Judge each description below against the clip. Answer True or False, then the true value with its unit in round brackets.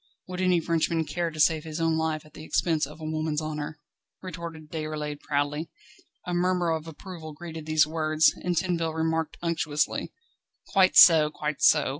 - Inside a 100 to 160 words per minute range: False (170 wpm)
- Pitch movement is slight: True (1.6 semitones)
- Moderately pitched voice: True (160 Hz)